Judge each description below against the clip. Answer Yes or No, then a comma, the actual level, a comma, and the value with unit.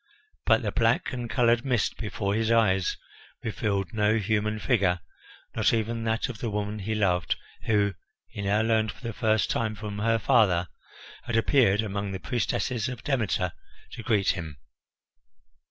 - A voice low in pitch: Yes, low, 110 Hz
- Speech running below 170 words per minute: Yes, average, 160 wpm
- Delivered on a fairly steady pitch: Yes, narrow, 2.3 semitones